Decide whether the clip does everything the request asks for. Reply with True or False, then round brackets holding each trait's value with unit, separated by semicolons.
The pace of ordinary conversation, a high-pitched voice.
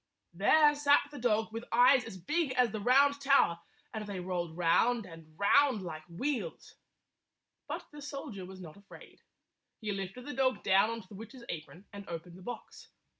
True (180 wpm; 215 Hz)